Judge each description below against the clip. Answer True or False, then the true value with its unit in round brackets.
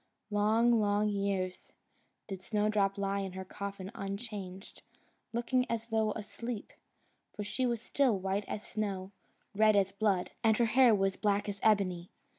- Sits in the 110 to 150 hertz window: False (205 Hz)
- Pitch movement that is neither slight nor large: False (2.1 semitones)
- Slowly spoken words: False (150 wpm)